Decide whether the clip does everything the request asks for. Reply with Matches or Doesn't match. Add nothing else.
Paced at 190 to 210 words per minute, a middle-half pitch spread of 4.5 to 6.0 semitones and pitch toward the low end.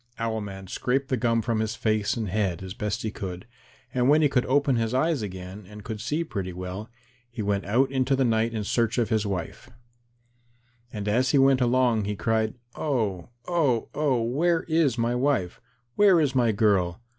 Doesn't match